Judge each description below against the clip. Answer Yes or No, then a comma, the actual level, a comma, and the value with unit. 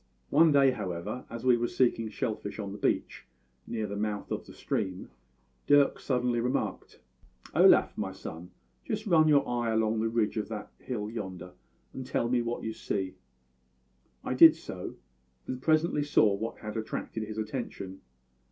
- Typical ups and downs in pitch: Yes, average, 3.6 semitones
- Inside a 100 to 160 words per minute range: No, average, 170 wpm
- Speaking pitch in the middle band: No, low, 115 Hz